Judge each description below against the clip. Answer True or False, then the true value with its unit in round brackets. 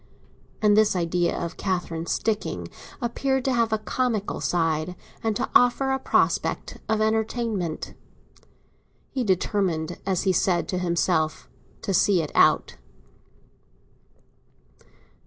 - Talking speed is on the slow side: True (120 wpm)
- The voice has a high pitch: True (195 Hz)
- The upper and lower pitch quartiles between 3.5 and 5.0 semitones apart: True (4.5 semitones)